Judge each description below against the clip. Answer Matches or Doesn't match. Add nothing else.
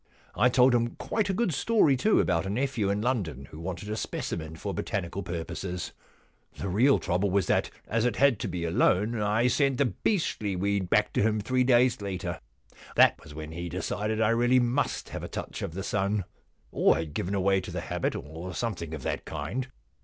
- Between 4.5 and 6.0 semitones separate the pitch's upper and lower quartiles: Matches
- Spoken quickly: Matches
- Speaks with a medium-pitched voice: Doesn't match